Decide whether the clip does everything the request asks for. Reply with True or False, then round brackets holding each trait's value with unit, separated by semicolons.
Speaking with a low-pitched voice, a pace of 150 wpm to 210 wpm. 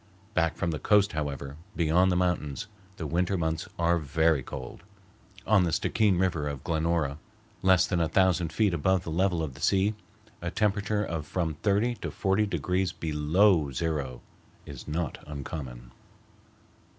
True (85 Hz; 155 wpm)